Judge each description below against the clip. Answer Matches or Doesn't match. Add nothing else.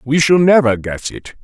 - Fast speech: Matches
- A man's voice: Matches